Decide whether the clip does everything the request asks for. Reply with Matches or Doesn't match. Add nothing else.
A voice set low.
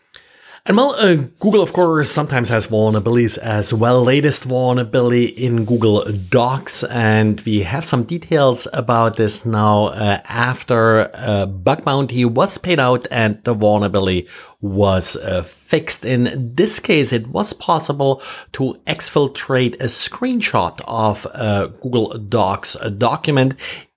Matches